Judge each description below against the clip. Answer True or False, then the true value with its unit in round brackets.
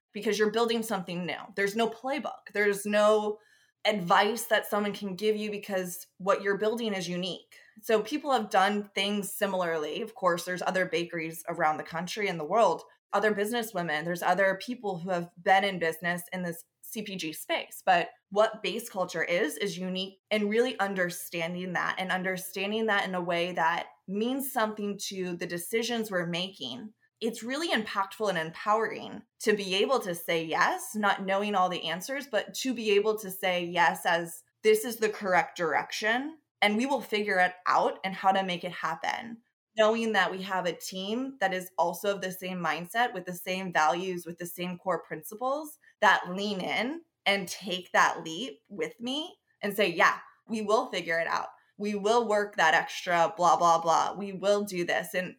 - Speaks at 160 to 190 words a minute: True (185 wpm)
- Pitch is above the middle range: True (195 Hz)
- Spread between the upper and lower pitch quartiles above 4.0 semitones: False (3.3 semitones)